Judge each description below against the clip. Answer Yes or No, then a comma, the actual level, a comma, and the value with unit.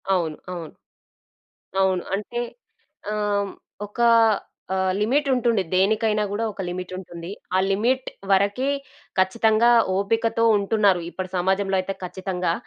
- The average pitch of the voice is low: No, high, 200 Hz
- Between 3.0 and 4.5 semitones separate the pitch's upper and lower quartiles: Yes, average, 3.3 semitones